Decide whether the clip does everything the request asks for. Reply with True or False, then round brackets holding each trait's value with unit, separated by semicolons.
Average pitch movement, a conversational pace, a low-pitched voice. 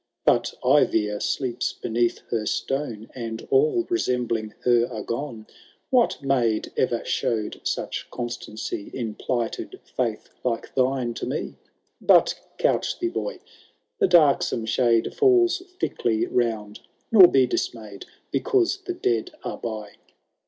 False (4.8 semitones; 125 wpm; 120 Hz)